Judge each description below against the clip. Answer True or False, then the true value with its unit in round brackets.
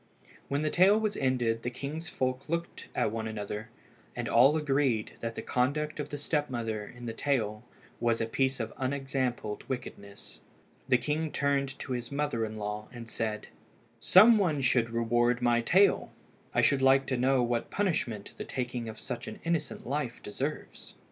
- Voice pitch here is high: False (130 Hz)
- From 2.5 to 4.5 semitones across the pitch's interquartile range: True (3.9 semitones)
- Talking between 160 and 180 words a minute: True (175 wpm)